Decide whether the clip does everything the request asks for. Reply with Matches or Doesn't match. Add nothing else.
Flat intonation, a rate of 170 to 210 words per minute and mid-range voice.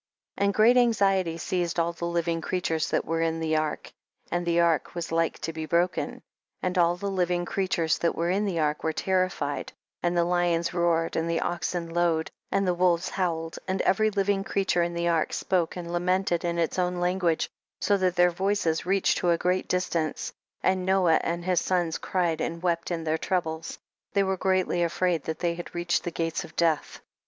Matches